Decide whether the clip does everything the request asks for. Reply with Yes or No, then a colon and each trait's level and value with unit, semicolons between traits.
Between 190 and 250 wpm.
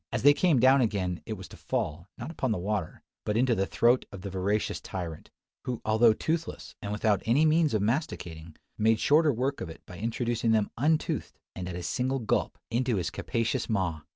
Yes: fast, 205 wpm